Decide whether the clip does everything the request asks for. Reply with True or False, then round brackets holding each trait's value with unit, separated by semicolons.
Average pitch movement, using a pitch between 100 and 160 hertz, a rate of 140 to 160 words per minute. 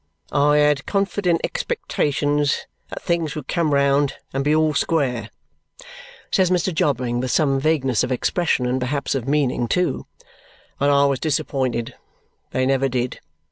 True (3.2 semitones; 140 Hz; 145 wpm)